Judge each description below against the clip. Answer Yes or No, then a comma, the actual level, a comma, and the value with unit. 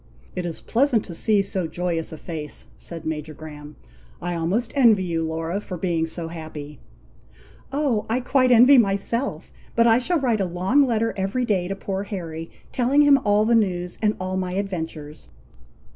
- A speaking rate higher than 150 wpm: Yes, average, 175 wpm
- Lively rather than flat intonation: Yes, wide, 5.8 semitones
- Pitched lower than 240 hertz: Yes, high, 190 Hz